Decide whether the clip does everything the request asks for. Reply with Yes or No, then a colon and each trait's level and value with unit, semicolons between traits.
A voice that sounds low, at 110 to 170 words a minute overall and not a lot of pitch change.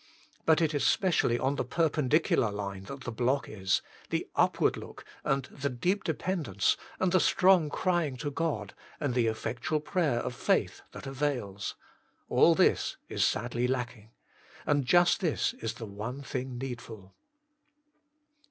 No: low, 130 Hz; average, 150 wpm; average, 4.9 semitones